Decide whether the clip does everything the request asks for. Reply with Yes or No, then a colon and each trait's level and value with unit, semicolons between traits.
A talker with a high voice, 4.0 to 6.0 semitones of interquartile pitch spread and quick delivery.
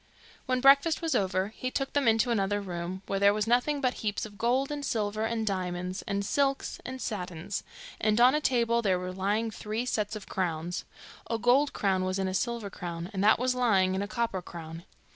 Yes: high, 210 Hz; average, 4.5 semitones; fast, 210 wpm